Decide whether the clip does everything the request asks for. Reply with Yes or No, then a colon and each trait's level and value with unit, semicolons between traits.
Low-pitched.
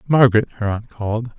Yes: low, 115 Hz